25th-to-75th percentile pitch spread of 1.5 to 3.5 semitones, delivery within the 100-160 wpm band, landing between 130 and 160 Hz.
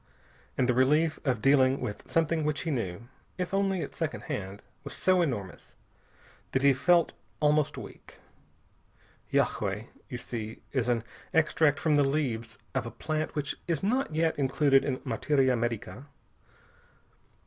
No: average, 4.1 semitones; average, 150 wpm; medium, 140 Hz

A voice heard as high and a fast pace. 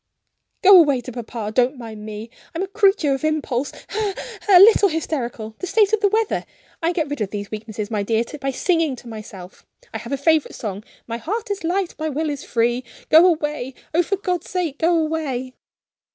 Yes: very high, 295 Hz; fast, 210 wpm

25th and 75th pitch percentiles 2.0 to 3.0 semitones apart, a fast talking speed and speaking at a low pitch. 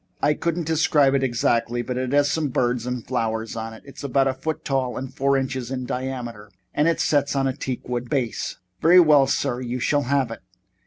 Yes: average, 2.7 semitones; fast, 210 wpm; low, 130 Hz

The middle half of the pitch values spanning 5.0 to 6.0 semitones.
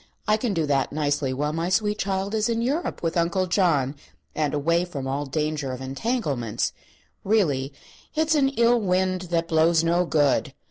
Yes: wide, 5.6 semitones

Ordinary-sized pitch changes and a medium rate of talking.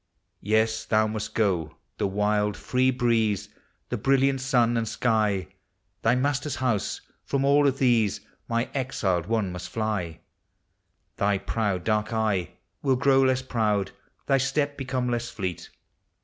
Yes: average, 4.0 semitones; average, 145 wpm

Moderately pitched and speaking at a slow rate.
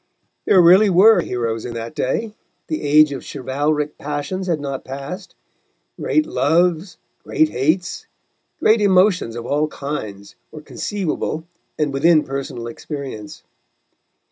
Yes: medium, 150 Hz; slow, 125 wpm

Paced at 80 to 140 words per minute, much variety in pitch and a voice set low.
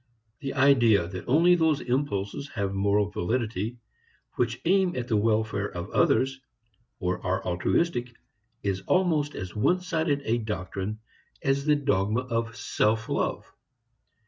Yes: slow, 135 wpm; wide, 5.8 semitones; low, 115 Hz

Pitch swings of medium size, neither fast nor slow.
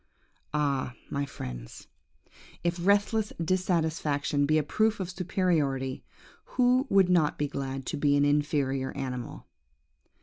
No: average, 4.7 semitones; slow, 125 wpm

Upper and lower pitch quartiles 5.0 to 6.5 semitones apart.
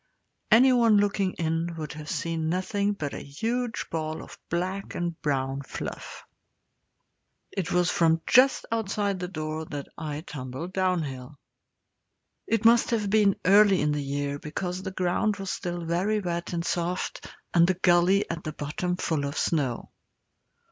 No: average, 4.2 semitones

